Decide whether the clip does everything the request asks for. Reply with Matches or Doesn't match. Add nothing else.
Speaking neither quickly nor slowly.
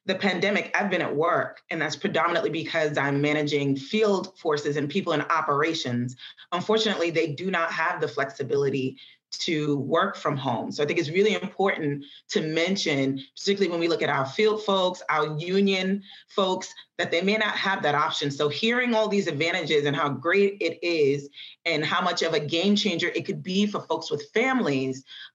Matches